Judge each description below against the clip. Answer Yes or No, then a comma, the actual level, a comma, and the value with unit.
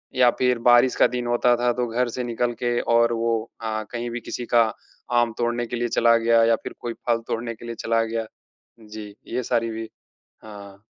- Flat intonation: Yes, narrow, 1.0 semitones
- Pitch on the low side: Yes, low, 115 Hz